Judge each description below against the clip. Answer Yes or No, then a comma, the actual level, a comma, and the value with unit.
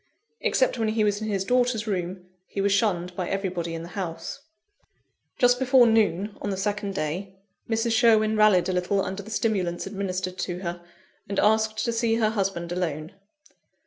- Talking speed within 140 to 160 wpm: No, average, 175 wpm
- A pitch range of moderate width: Yes, average, 3.3 semitones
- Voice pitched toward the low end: No, high, 200 Hz